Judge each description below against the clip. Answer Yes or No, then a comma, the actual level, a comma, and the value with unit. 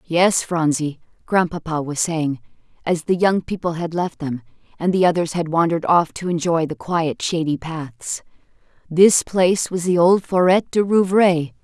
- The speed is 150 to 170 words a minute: Yes, average, 165 wpm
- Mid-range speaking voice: Yes, medium, 170 Hz